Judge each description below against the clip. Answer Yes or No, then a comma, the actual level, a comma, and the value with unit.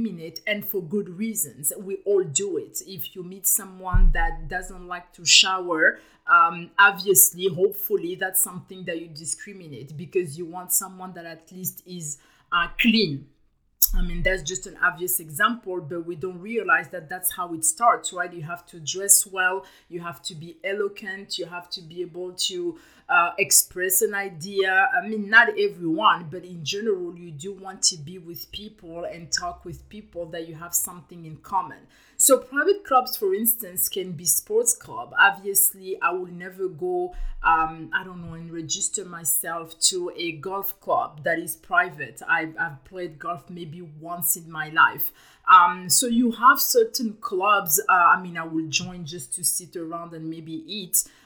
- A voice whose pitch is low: No, medium, 180 Hz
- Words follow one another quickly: No, average, 180 wpm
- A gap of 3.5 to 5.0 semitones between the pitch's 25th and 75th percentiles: No, average, 3.0 semitones